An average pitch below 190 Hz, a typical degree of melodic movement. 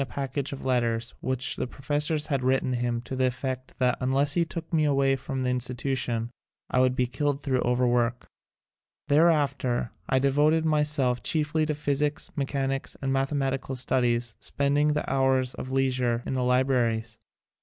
No: low, 135 Hz; narrow, 2.2 semitones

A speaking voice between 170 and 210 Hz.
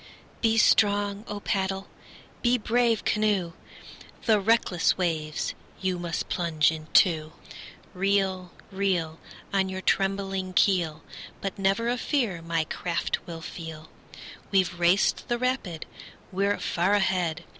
Yes: high, 190 Hz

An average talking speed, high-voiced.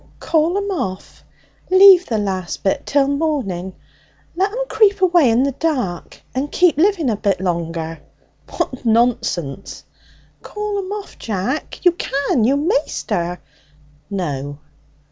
No: slow, 130 wpm; very high, 265 Hz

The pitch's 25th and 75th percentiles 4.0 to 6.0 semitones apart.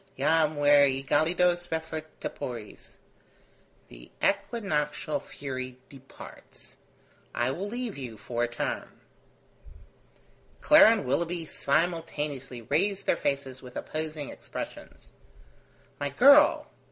Yes: average, 4.8 semitones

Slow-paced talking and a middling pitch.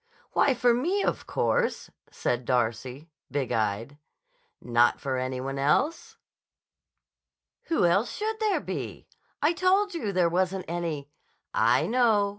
Yes: slow, 130 wpm; medium, 175 Hz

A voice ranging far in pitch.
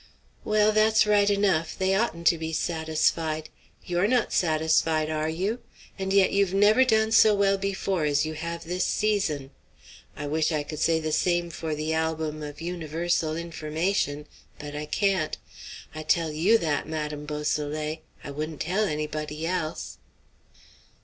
No: average, 4.0 semitones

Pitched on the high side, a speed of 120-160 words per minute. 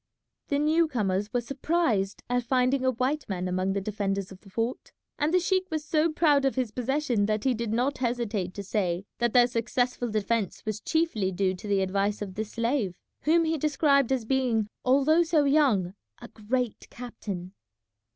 No: high, 240 Hz; average, 185 wpm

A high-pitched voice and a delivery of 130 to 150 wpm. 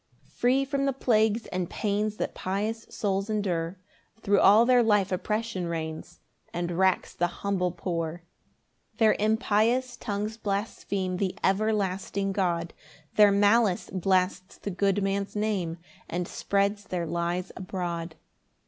Yes: high, 200 Hz; slow, 135 wpm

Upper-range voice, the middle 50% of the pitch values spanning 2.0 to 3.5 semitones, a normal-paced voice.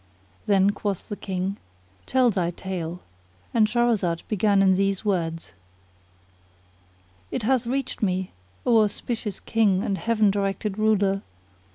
No: high, 200 Hz; narrow, 2.5 semitones; slow, 125 wpm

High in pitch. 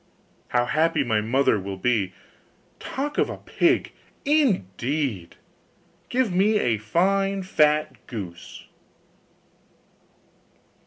No: medium, 145 Hz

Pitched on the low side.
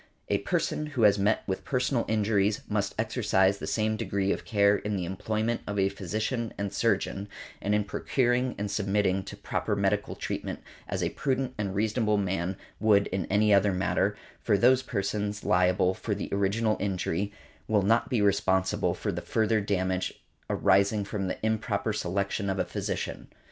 Yes: low, 100 Hz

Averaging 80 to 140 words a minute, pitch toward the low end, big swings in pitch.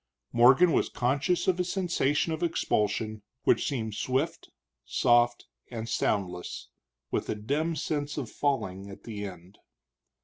Yes: slow, 135 wpm; low, 125 Hz; wide, 6.5 semitones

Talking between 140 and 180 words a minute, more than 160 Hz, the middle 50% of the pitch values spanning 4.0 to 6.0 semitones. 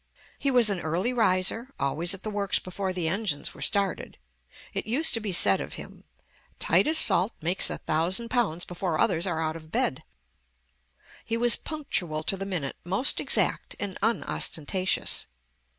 Yes: average, 165 wpm; high, 190 Hz; average, 5.1 semitones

